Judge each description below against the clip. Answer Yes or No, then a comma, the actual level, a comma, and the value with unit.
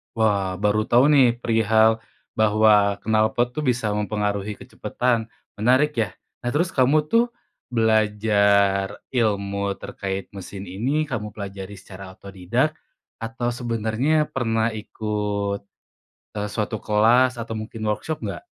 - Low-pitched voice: Yes, low, 110 Hz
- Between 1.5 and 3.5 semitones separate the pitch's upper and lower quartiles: Yes, average, 2.9 semitones